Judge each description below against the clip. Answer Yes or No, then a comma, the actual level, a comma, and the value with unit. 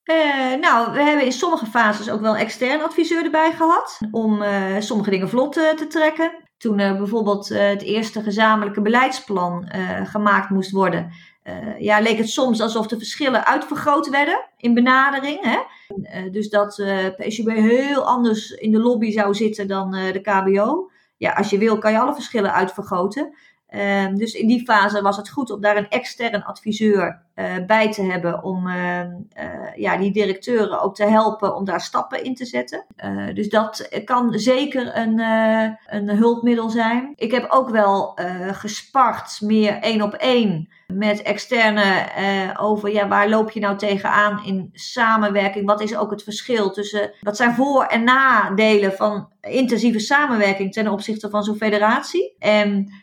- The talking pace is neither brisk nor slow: Yes, average, 175 wpm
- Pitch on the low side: No, high, 215 Hz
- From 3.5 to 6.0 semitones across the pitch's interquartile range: No, average, 3.0 semitones